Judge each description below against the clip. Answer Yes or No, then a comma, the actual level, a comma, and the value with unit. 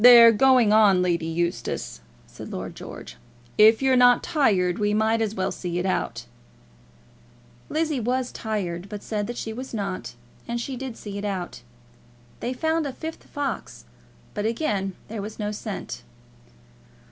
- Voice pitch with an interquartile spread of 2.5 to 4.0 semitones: No, average, 4.4 semitones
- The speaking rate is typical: Yes, average, 160 wpm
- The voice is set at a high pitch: Yes, high, 215 Hz